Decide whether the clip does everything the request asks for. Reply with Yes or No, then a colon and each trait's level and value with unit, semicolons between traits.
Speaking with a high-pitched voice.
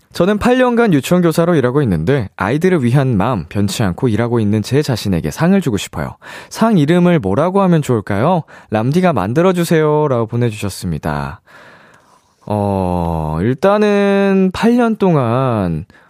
No: low, 135 Hz